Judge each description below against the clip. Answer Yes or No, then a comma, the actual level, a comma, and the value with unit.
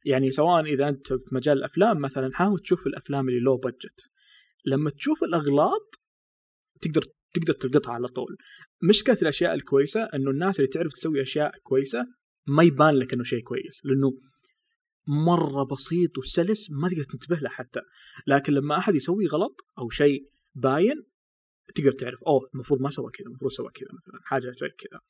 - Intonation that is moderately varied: Yes, average, 4.6 semitones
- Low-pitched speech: No, medium, 145 Hz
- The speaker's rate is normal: No, fast, 165 wpm